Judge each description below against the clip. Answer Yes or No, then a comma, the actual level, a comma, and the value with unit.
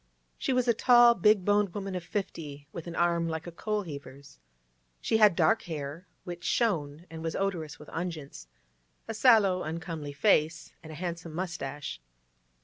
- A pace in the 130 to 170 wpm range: Yes, average, 160 wpm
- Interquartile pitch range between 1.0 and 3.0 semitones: No, average, 4.4 semitones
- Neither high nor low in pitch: Yes, medium, 170 Hz